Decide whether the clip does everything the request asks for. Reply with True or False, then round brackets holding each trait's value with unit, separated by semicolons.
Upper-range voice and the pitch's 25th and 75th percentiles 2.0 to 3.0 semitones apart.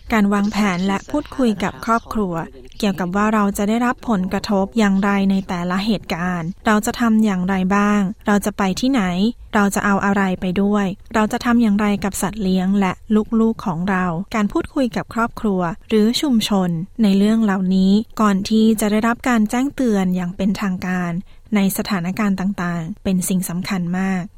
True (200 Hz; 2.5 semitones)